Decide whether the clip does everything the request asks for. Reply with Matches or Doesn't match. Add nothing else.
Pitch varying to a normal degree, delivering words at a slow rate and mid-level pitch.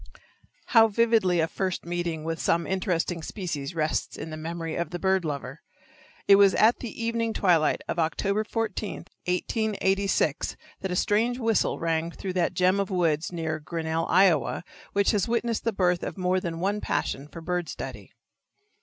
Doesn't match